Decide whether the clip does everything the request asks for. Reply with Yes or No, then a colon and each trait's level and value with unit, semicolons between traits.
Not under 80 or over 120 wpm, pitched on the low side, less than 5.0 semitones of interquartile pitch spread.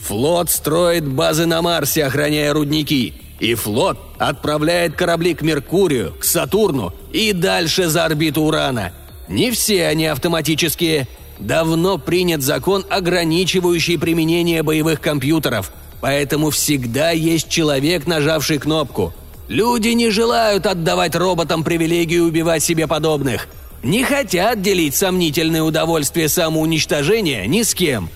No: average, 115 wpm; medium, 165 Hz; narrow, 2.4 semitones